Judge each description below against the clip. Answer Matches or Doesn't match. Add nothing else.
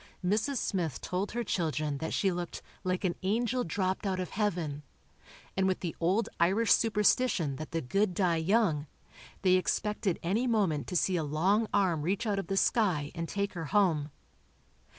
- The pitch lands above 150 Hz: Matches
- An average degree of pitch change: Matches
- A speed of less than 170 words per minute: Doesn't match